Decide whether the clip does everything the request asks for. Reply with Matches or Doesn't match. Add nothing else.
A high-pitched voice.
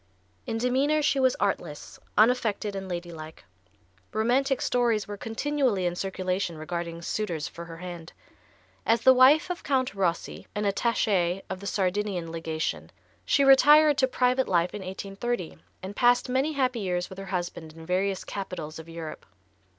Matches